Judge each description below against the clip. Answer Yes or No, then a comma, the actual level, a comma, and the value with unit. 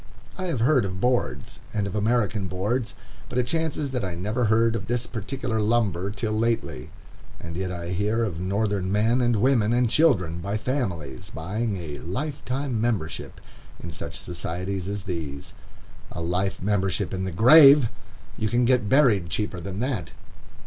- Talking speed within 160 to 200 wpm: Yes, average, 165 wpm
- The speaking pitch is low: Yes, low, 105 Hz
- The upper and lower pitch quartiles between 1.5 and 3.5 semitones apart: No, average, 4.8 semitones